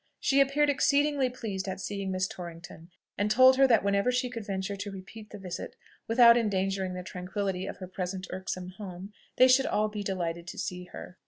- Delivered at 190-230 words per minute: Yes, average, 195 wpm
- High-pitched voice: Yes, high, 200 Hz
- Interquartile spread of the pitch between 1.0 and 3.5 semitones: No, average, 4.1 semitones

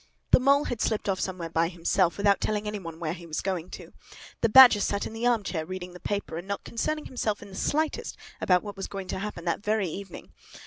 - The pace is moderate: No, fast, 240 wpm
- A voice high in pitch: Yes, high, 200 Hz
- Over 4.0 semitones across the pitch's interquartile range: No, average, 3.3 semitones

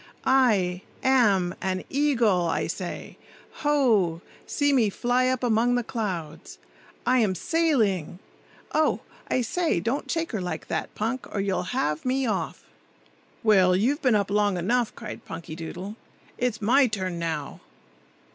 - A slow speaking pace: Yes, slow, 130 wpm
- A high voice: Yes, high, 215 Hz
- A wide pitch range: Yes, wide, 5.7 semitones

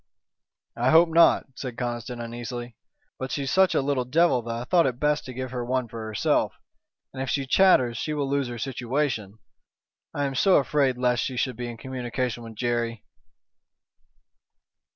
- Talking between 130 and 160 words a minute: No, average, 175 wpm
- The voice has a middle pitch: No, low, 125 Hz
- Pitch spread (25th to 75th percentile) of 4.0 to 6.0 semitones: No, average, 2.7 semitones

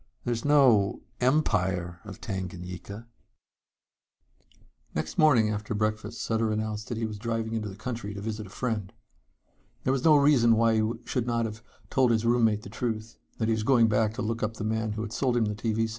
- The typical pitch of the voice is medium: No, low, 110 Hz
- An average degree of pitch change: No, narrow, 1.8 semitones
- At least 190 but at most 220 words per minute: Yes, average, 195 wpm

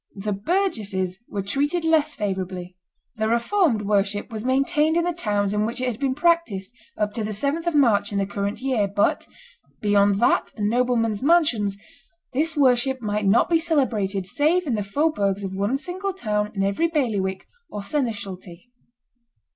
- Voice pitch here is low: No, high, 220 Hz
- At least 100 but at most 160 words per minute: No, average, 170 wpm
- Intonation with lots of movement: Yes, wide, 6.5 semitones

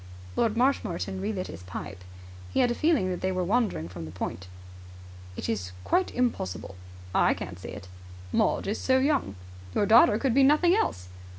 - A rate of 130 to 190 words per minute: Yes, average, 180 wpm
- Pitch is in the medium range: No, high, 195 Hz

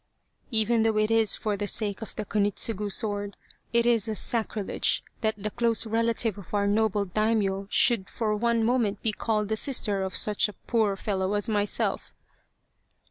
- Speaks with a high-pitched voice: Yes, high, 215 Hz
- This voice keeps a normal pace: Yes, average, 180 wpm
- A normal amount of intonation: No, narrow, 1.8 semitones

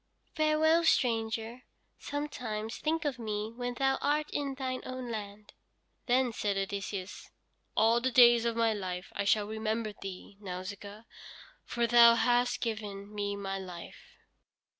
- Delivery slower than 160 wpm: Yes, average, 140 wpm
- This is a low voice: No, high, 225 Hz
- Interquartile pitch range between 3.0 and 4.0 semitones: Yes, average, 3.7 semitones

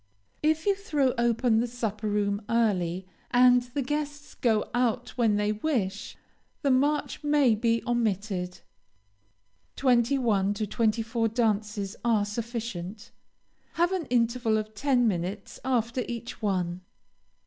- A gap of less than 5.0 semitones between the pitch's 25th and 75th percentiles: Yes, average, 3.3 semitones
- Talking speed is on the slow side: Yes, slow, 130 wpm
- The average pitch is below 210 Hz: No, high, 230 Hz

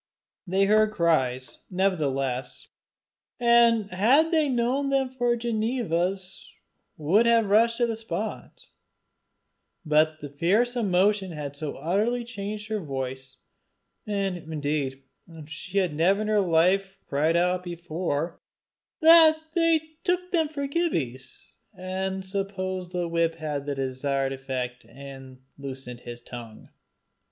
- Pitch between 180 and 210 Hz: Yes, medium, 185 Hz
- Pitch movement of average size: No, wide, 7.6 semitones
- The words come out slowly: Yes, slow, 125 wpm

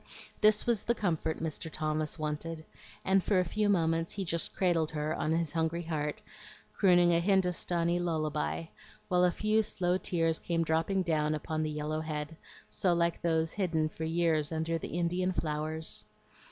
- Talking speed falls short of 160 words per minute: No, average, 165 wpm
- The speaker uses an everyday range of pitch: No, narrow, 2.2 semitones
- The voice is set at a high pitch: No, medium, 165 Hz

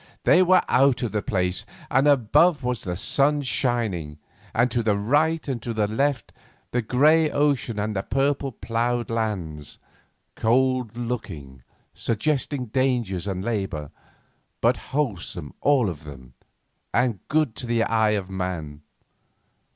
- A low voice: Yes, low, 115 Hz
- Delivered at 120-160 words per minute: Yes, slow, 135 wpm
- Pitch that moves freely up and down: Yes, wide, 5.7 semitones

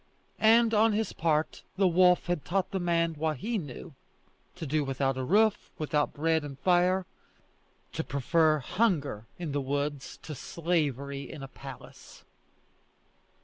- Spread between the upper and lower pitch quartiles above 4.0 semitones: Yes, average, 4.4 semitones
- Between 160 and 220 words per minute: No, average, 145 wpm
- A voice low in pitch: No, medium, 160 Hz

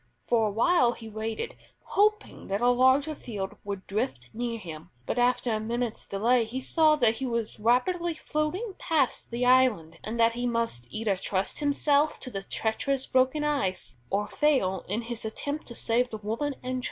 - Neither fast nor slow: Yes, average, 180 wpm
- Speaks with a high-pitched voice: Yes, high, 240 Hz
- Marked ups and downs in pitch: No, average, 4.0 semitones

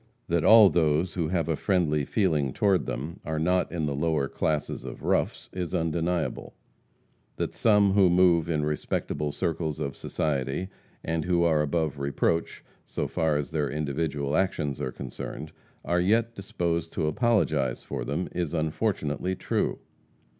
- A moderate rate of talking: Yes, average, 155 wpm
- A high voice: No, very low, 80 Hz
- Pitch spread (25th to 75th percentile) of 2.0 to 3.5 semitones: Yes, average, 3.2 semitones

